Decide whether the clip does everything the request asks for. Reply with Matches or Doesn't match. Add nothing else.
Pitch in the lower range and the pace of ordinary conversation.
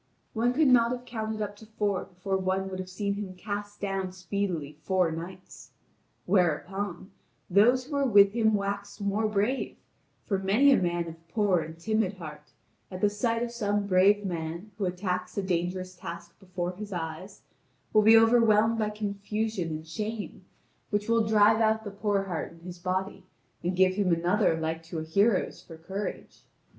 Doesn't match